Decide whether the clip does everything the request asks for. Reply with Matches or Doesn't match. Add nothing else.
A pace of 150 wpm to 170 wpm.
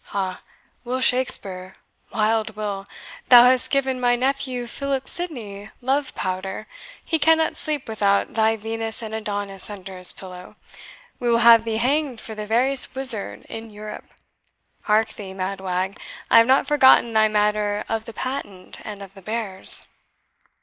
Matches